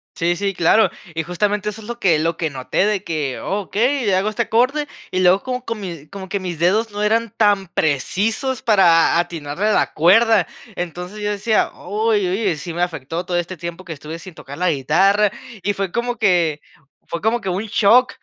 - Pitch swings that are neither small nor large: Yes, average, 3.9 semitones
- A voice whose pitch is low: No, high, 190 Hz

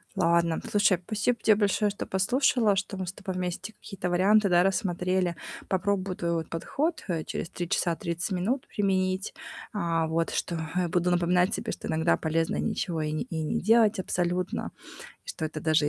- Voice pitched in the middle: Yes, medium, 180 Hz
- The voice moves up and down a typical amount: Yes, average, 3.0 semitones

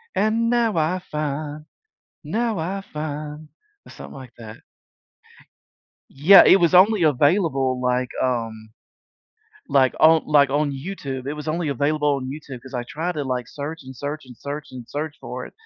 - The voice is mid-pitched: Yes, medium, 150 Hz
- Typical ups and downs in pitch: Yes, average, 3.5 semitones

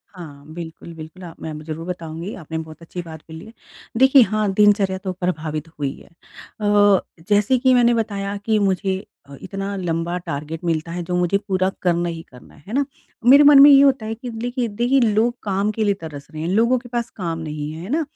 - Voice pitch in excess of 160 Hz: Yes, high, 190 Hz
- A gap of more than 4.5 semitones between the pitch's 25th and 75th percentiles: Yes, average, 5.1 semitones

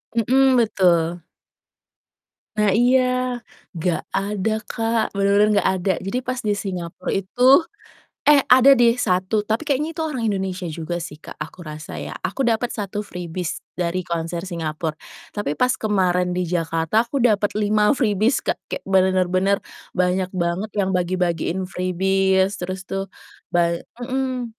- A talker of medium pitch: No, high, 195 Hz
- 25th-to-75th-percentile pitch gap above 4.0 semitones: Yes, average, 4.4 semitones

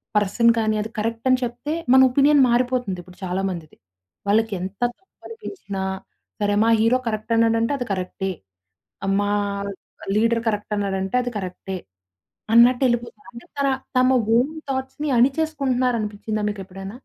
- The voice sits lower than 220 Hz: No, high, 230 Hz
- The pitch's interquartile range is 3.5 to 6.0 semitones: Yes, average, 3.9 semitones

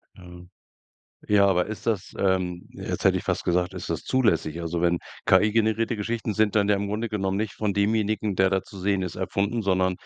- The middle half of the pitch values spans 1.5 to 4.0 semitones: Yes, average, 2.9 semitones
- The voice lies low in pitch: Yes, low, 100 Hz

